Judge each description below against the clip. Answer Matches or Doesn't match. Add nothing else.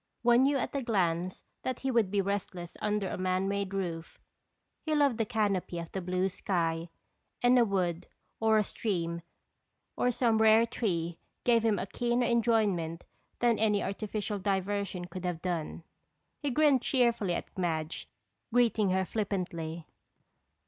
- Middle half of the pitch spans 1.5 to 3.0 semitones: Doesn't match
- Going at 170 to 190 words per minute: Doesn't match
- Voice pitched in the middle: Doesn't match